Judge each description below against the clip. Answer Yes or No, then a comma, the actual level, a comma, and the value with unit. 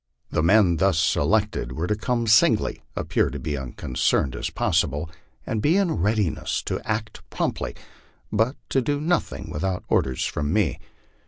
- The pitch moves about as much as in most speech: No, wide, 6.2 semitones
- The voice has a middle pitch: No, very low, 95 Hz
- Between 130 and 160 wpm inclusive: Yes, average, 150 wpm